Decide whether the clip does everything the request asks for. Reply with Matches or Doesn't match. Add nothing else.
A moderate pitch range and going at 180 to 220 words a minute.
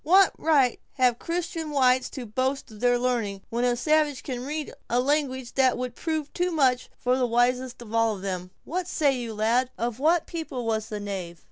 Matches